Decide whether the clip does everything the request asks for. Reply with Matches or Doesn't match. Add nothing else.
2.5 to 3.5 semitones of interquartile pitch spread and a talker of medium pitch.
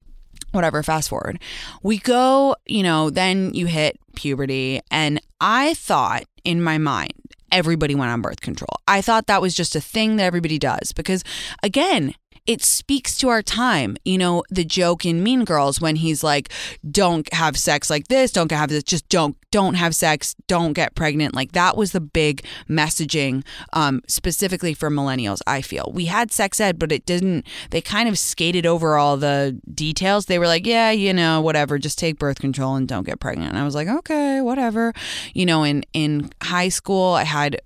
Doesn't match